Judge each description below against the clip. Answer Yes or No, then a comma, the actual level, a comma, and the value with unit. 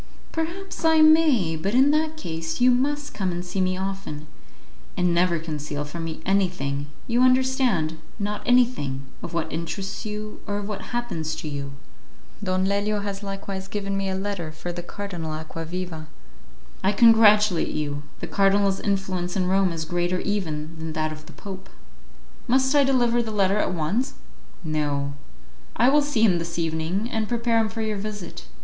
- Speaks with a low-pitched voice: No, high, 195 Hz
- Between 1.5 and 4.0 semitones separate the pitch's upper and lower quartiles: No, wide, 5.4 semitones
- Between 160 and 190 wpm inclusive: Yes, average, 170 wpm